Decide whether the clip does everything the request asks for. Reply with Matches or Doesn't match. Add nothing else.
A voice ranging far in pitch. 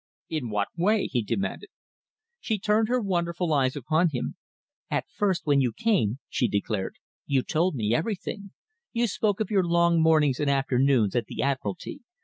Matches